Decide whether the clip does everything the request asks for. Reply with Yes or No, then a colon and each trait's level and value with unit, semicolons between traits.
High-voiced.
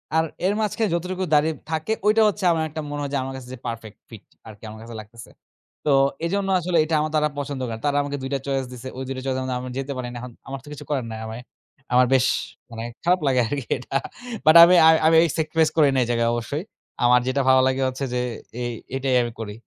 No: low, 135 Hz